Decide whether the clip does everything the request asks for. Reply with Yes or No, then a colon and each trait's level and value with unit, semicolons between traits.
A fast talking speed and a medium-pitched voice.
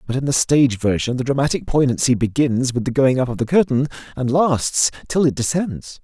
No: fast, 210 wpm; low, 130 Hz